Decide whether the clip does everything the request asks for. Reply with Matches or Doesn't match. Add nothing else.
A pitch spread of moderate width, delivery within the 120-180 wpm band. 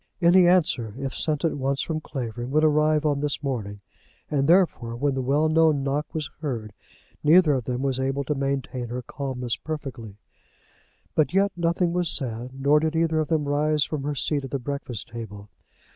Doesn't match